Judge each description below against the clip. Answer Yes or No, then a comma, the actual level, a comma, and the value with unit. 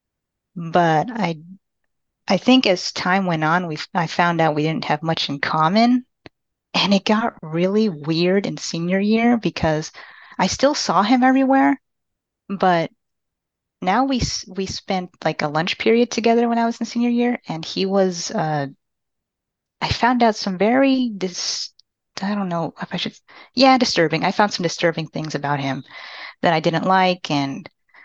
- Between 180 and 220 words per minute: No, average, 165 wpm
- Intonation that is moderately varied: No, wide, 5.9 semitones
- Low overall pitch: No, medium, 185 Hz